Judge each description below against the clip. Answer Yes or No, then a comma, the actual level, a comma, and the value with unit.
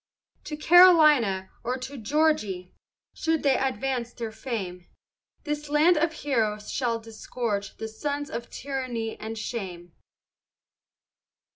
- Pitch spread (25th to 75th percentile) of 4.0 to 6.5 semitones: Yes, average, 5.1 semitones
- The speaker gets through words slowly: Yes, slow, 120 wpm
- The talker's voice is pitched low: No, high, 245 Hz